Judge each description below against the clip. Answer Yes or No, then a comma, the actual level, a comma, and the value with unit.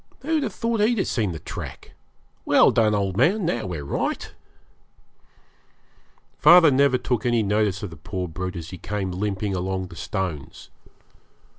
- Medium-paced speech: Yes, average, 160 wpm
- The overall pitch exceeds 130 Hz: No, low, 105 Hz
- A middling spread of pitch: No, wide, 6.7 semitones